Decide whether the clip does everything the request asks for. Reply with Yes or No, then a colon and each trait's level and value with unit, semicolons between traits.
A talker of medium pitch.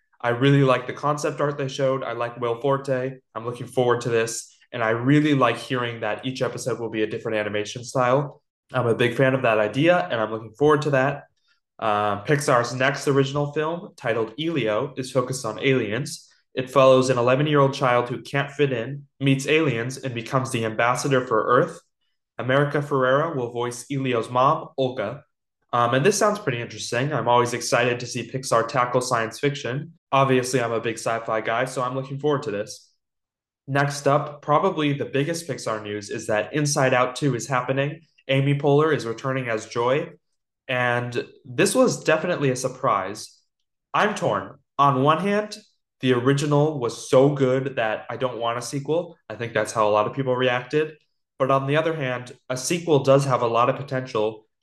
No: low, 130 Hz